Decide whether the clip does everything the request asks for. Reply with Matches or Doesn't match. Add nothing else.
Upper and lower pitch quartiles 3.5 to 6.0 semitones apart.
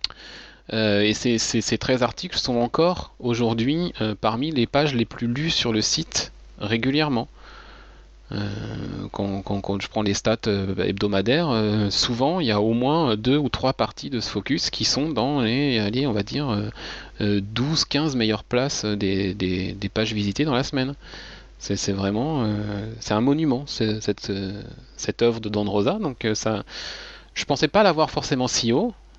Matches